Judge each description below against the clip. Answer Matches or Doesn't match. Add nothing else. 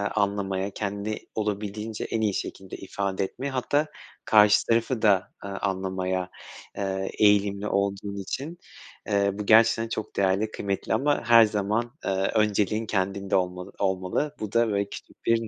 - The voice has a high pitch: Doesn't match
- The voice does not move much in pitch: Matches